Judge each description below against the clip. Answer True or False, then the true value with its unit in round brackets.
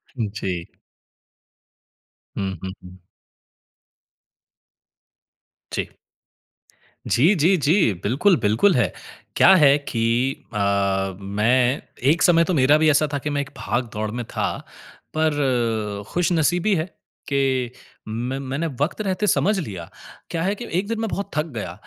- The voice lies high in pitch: False (135 Hz)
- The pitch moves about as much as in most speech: False (6.9 semitones)